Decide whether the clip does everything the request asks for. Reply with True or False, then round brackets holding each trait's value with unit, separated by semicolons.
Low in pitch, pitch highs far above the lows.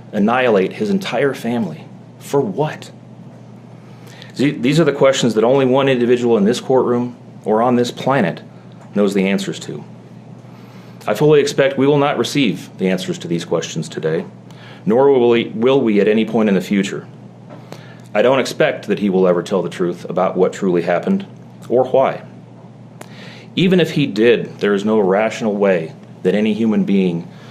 True (115 Hz; 6.9 semitones)